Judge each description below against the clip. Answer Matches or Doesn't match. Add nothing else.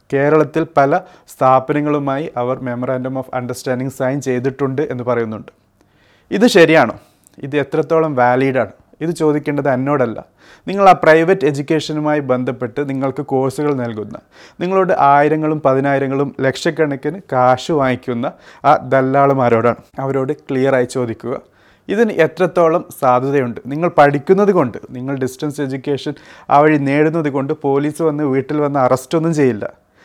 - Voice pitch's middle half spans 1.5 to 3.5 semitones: Matches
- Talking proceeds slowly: Doesn't match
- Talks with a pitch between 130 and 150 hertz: Matches